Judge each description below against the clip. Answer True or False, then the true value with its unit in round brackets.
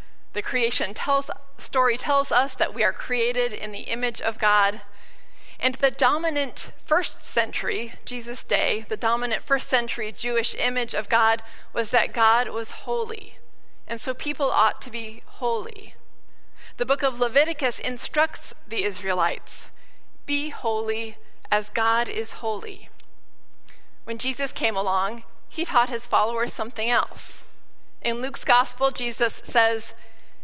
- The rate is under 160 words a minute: True (140 wpm)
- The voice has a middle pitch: False (235 Hz)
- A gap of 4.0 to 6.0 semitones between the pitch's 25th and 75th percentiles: False (3.3 semitones)